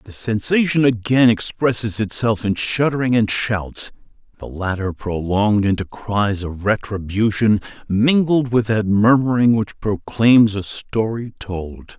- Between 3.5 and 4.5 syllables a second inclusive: Yes, 4.1 syllables/s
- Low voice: Yes, low, 110 Hz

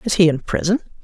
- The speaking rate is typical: No, fast, 230 wpm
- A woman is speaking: Yes, female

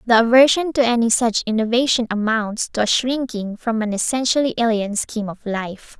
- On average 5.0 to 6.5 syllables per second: Yes, 5.4 syllables/s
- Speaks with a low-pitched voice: No, high, 230 Hz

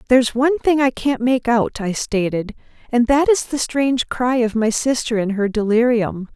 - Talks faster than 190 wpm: Yes, average, 200 wpm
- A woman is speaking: Yes, female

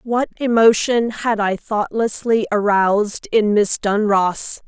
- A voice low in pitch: No, high, 215 Hz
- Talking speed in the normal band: No, slow, 115 wpm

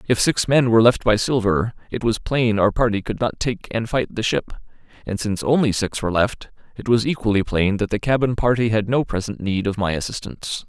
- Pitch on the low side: Yes, low, 110 Hz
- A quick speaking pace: Yes, fast, 225 wpm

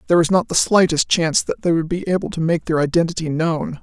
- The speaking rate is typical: No, fast, 250 wpm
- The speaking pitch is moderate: Yes, medium, 165 Hz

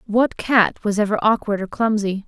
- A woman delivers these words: Yes, female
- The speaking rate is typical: Yes, average, 185 wpm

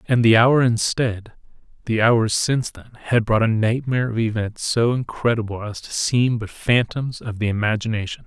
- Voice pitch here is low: Yes, low, 115 Hz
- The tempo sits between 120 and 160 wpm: No, average, 175 wpm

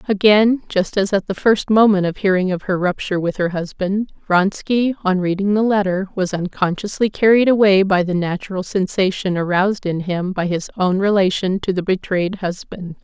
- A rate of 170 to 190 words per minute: Yes, average, 180 wpm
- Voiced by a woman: Yes, female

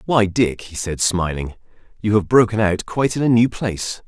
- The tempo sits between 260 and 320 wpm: No, fast, 205 wpm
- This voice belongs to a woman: No, male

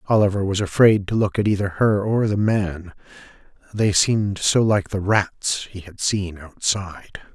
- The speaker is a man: Yes, male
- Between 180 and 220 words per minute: No, average, 170 wpm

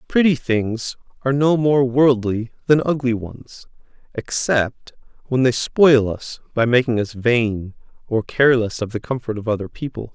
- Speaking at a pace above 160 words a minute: No, average, 155 wpm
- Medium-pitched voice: No, low, 125 Hz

